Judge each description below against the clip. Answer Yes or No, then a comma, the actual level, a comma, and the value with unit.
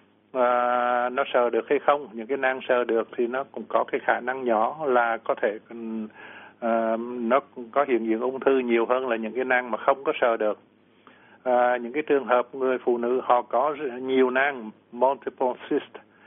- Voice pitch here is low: Yes, low, 125 Hz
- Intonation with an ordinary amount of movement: No, narrow, 2.1 semitones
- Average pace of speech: Yes, average, 200 wpm